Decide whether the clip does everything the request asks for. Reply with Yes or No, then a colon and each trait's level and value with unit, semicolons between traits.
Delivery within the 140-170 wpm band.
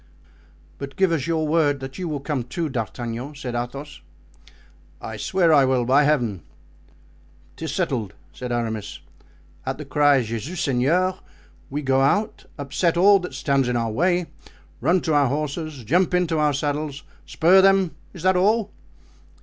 Yes: average, 155 wpm